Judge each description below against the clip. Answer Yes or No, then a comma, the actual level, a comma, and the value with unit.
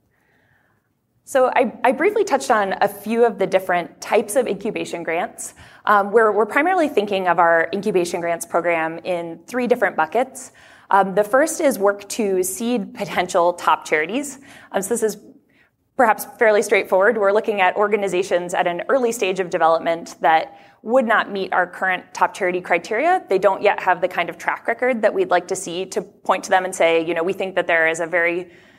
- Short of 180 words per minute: No, average, 195 wpm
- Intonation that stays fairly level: No, average, 4.2 semitones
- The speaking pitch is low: No, high, 195 Hz